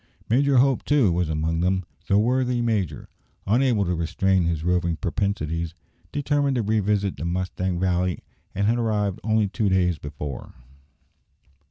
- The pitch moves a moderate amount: Yes, average, 4.6 semitones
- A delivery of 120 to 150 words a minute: Yes, average, 145 wpm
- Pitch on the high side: No, very low, 95 Hz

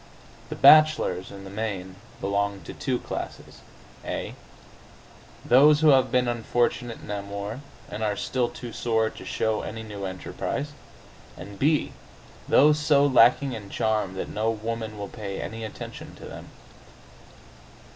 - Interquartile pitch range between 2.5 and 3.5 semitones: No, average, 3.9 semitones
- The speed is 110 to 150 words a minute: Yes, average, 145 wpm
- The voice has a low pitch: Yes, low, 110 Hz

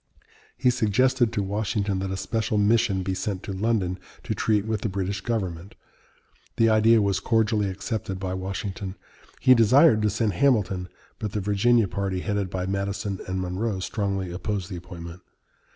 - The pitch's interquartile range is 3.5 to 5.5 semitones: No, average, 2.8 semitones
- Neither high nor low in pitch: No, low, 100 Hz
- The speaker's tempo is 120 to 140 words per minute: No, average, 165 wpm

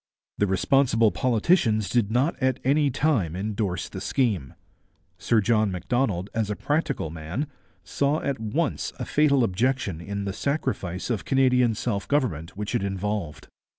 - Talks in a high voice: No, low, 110 Hz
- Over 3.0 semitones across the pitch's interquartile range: Yes, wide, 5.5 semitones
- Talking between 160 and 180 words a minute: No, average, 150 wpm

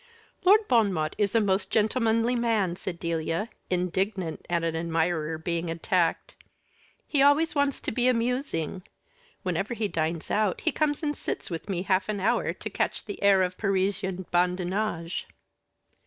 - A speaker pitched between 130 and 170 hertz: No, high, 190 Hz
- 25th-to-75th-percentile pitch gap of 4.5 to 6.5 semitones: Yes, average, 4.9 semitones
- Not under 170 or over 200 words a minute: No, average, 155 wpm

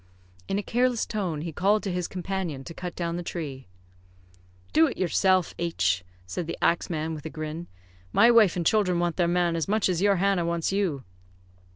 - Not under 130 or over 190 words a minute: No, fast, 205 wpm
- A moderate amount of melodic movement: Yes, average, 3.2 semitones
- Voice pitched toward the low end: No, medium, 175 Hz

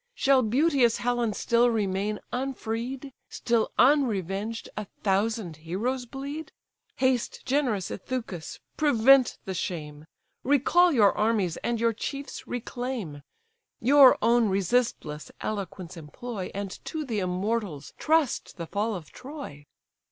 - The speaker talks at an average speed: No, slow, 115 wpm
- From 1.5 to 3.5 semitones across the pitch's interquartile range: No, average, 5.1 semitones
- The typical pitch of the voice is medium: No, high, 230 Hz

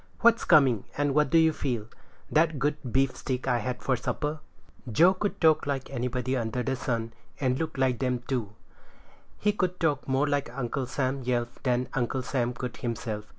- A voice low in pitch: Yes, low, 130 Hz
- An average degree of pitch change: Yes, average, 3.2 semitones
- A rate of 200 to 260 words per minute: No, average, 175 wpm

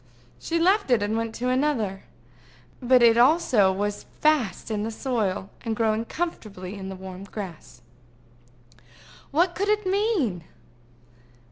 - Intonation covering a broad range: Yes, wide, 7.3 semitones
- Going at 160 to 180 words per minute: No, slow, 135 wpm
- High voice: Yes, high, 225 Hz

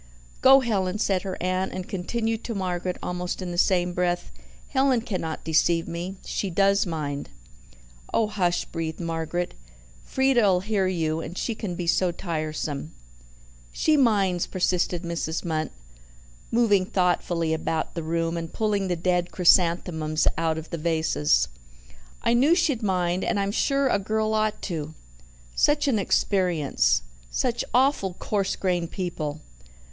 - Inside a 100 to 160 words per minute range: Yes, average, 145 wpm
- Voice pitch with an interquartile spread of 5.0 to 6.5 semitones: No, average, 3.7 semitones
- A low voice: No, medium, 180 Hz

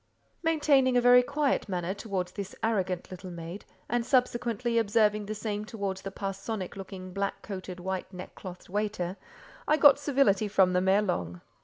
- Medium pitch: No, high, 200 Hz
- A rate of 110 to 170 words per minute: Yes, average, 160 wpm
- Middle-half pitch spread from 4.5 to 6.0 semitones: No, average, 4.0 semitones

